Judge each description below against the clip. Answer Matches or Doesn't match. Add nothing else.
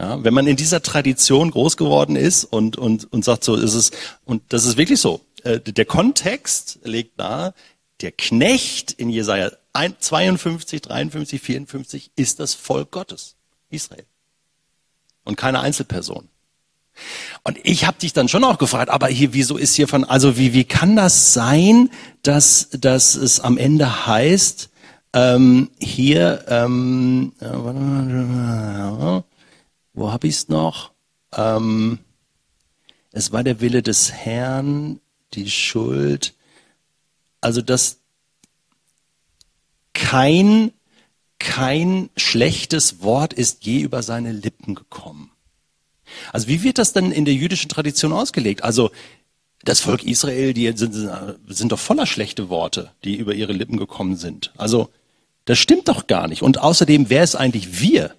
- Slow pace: Doesn't match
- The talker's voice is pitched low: Matches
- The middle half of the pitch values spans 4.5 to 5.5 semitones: Matches